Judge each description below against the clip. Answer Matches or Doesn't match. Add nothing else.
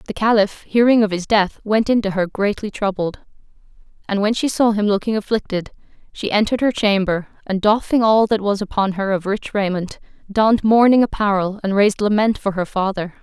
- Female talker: Matches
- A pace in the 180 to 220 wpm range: Matches